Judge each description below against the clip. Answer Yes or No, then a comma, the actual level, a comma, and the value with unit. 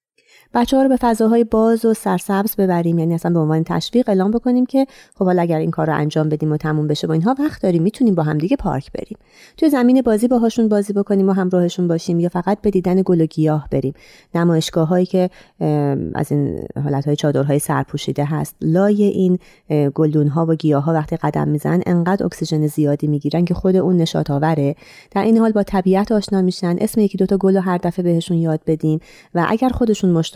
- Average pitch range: Yes, average, 4.6 semitones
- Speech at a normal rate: No, fast, 210 wpm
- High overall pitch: No, medium, 175 Hz